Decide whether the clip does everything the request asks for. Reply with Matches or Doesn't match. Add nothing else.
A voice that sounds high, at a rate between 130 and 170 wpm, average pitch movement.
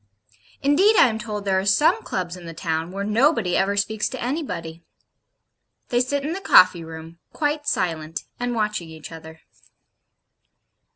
Doesn't match